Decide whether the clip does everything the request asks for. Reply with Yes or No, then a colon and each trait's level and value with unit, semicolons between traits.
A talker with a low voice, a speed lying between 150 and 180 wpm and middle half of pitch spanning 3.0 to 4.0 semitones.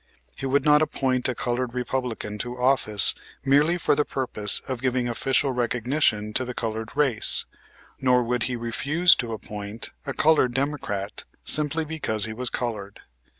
Yes: low, 125 Hz; average, 155 wpm; average, 3.3 semitones